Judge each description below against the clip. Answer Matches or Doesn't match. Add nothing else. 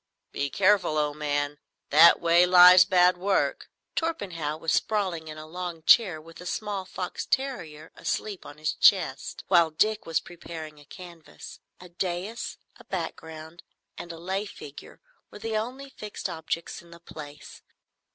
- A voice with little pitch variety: Doesn't match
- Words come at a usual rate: Matches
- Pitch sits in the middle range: Matches